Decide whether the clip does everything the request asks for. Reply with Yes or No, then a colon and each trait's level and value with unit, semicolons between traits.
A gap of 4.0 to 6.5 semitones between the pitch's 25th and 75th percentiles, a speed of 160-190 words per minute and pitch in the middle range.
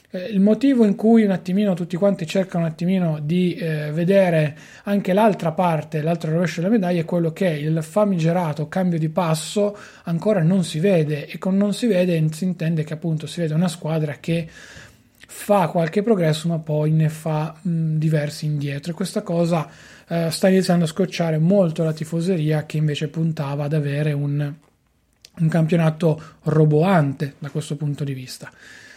No: average, 3.2 semitones; fast, 170 wpm; medium, 165 Hz